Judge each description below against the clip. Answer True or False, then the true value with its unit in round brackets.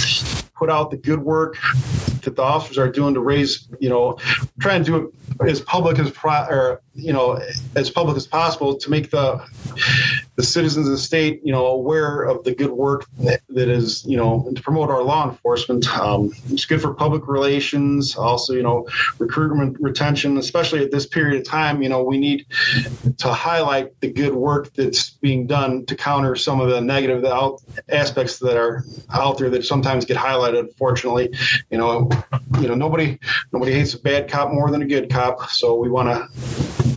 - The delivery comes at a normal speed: True (190 wpm)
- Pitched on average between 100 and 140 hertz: True (135 Hz)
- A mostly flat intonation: True (2.3 semitones)